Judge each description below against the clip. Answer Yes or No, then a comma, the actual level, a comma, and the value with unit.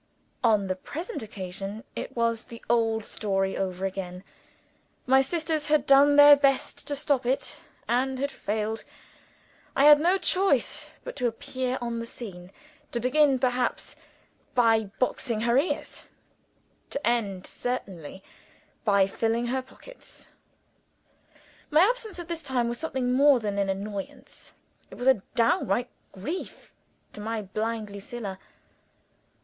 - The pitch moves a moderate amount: Yes, average, 5.0 semitones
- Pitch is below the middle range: No, high, 240 Hz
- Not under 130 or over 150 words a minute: Yes, slow, 135 wpm